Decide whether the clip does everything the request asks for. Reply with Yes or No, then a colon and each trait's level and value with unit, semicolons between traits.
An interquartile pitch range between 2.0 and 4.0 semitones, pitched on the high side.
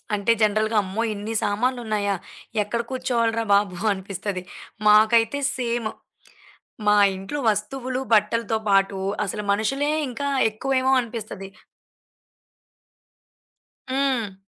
Yes: average, 3.2 semitones; high, 220 Hz